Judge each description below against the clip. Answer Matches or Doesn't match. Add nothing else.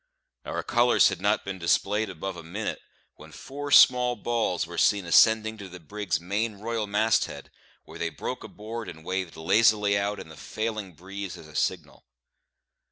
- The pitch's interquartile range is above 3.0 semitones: Matches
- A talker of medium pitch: Doesn't match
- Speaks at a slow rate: Doesn't match